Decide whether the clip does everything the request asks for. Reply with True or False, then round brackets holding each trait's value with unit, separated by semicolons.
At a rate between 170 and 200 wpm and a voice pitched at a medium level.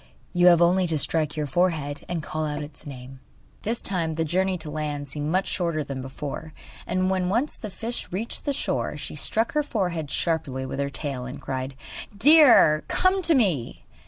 True (190 wpm; 160 Hz)